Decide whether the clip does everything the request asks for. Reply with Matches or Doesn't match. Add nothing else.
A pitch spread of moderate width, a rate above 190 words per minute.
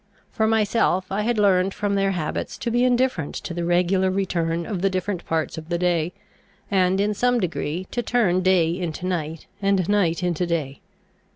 Doesn't match